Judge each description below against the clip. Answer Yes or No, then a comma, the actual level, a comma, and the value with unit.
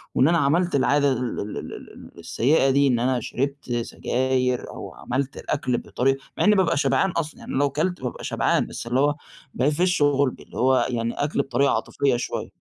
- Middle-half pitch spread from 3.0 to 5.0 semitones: No, narrow, 2.5 semitones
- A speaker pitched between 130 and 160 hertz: Yes, low, 135 Hz